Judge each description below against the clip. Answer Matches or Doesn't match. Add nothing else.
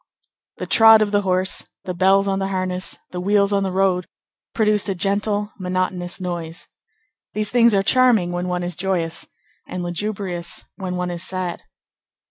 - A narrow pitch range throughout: Matches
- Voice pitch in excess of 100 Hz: Matches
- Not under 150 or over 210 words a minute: Matches